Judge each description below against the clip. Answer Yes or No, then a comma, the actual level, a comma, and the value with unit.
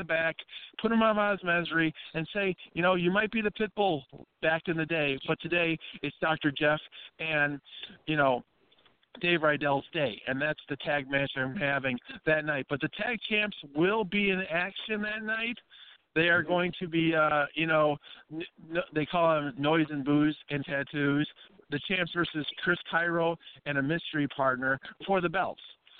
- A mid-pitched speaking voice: Yes, medium, 160 Hz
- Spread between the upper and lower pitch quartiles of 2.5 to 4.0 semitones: Yes, average, 3.6 semitones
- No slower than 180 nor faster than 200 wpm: Yes, average, 185 wpm